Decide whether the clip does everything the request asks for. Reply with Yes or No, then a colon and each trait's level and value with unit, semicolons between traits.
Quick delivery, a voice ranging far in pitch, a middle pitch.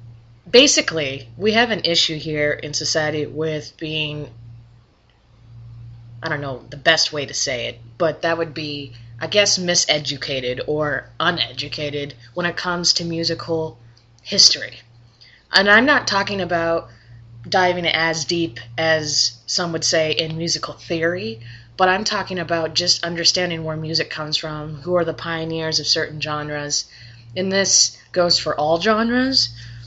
No: average, 145 wpm; wide, 5.7 semitones; medium, 155 Hz